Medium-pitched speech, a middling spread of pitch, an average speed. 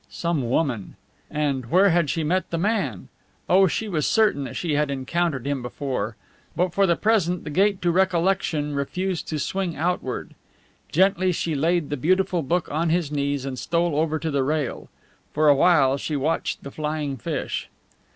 Yes: medium, 160 Hz; average, 4.1 semitones; average, 180 wpm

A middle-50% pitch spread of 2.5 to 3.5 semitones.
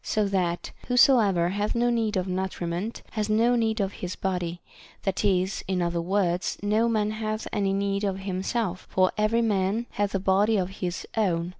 Yes: average, 2.8 semitones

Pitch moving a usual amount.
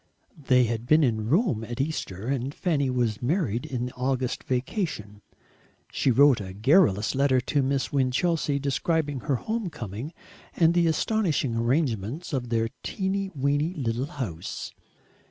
Yes: average, 4.8 semitones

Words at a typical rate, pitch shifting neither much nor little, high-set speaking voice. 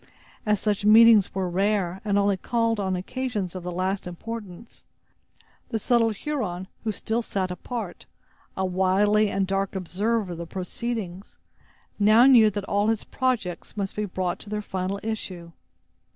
Yes: average, 155 wpm; average, 3.1 semitones; high, 200 Hz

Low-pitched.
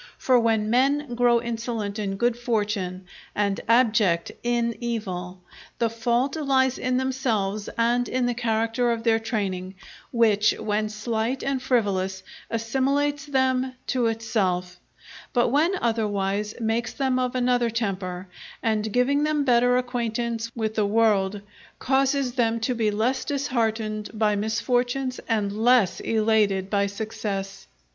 No: high, 230 Hz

